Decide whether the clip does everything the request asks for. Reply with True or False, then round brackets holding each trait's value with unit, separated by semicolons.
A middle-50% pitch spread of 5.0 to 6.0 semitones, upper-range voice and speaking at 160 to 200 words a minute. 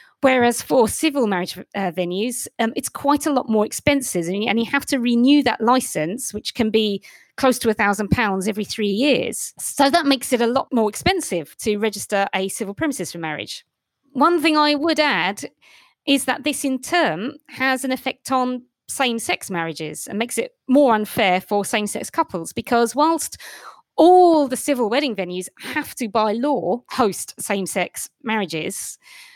True (5.5 semitones; 240 Hz; 180 wpm)